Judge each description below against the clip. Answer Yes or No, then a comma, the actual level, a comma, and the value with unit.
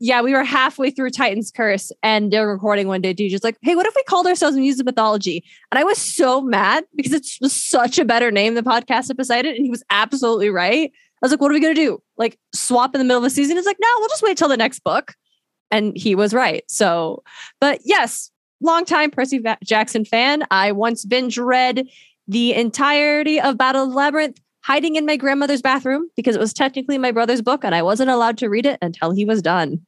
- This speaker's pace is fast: Yes, fast, 240 wpm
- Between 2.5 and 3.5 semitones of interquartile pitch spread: No, average, 4.4 semitones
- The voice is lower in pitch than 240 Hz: No, very high, 255 Hz